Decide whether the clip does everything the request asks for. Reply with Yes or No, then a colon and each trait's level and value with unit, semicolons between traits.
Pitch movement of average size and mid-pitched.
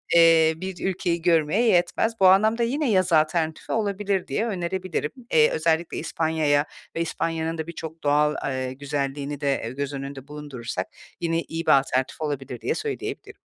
Yes: average, 3.5 semitones; medium, 160 Hz